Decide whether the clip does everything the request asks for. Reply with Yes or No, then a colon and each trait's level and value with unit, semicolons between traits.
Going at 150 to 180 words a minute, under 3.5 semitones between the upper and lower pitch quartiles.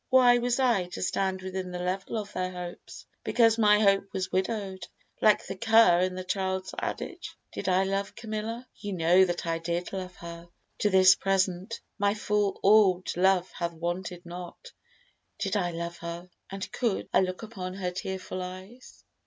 Yes: average, 175 wpm; narrow, 2.5 semitones